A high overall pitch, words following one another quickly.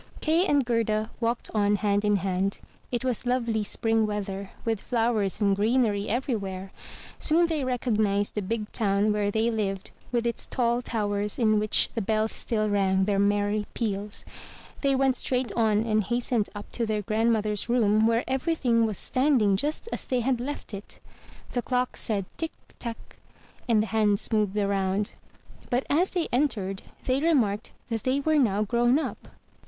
No: high, 220 Hz; average, 170 wpm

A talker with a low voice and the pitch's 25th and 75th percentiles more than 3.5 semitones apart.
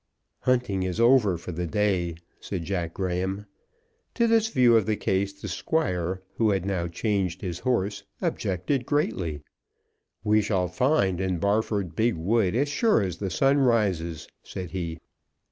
Yes: low, 100 Hz; average, 4.4 semitones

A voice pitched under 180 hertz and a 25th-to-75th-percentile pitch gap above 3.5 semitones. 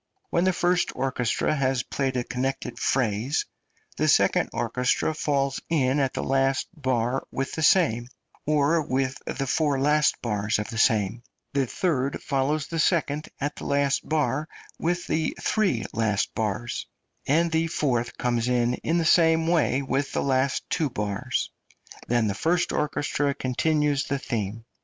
Yes: low, 135 Hz; average, 3.9 semitones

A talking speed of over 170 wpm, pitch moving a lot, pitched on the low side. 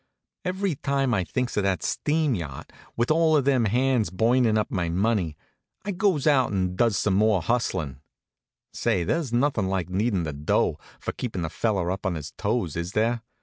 Yes: average, 185 wpm; wide, 6.1 semitones; low, 110 Hz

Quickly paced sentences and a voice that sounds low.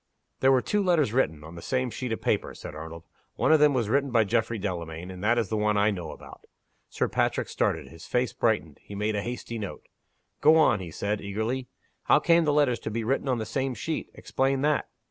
Yes: fast, 230 wpm; low, 115 Hz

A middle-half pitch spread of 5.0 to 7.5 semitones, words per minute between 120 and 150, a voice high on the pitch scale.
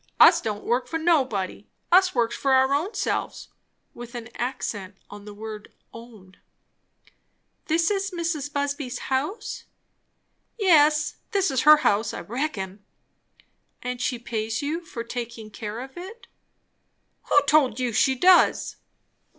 Yes: wide, 5.4 semitones; slow, 135 wpm; very high, 260 Hz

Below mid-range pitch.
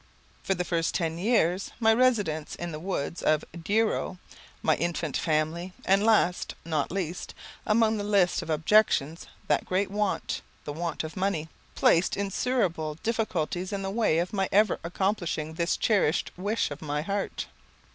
No: medium, 180 Hz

